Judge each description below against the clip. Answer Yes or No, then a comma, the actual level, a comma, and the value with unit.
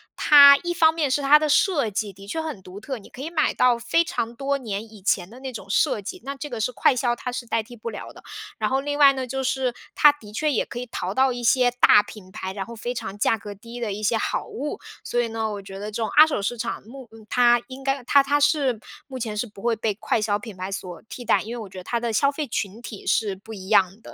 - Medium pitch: No, high, 235 Hz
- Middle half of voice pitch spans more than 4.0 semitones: Yes, average, 4.4 semitones